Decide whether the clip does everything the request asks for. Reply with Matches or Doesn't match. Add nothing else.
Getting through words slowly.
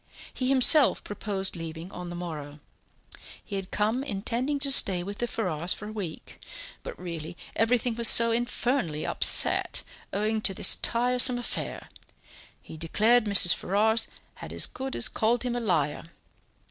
Doesn't match